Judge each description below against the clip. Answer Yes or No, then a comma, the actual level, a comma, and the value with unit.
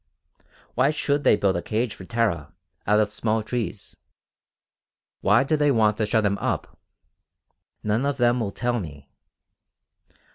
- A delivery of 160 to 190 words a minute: No, average, 150 wpm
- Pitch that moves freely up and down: No, average, 3.0 semitones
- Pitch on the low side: Yes, low, 110 Hz